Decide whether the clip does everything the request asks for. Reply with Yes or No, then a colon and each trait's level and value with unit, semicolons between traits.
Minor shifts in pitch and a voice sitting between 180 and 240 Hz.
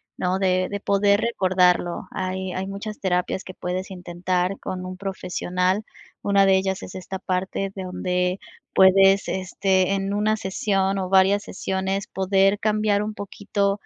Yes: narrow, 1.3 semitones; high, 190 Hz